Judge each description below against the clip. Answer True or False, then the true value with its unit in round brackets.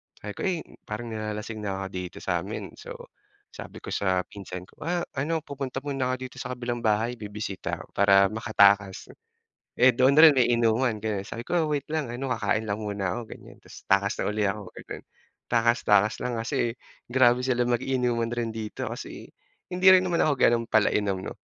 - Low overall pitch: True (115 Hz)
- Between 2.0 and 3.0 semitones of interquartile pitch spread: False (3.7 semitones)